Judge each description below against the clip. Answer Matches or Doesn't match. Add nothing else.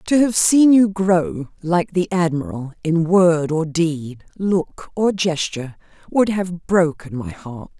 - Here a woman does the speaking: Matches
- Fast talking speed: Doesn't match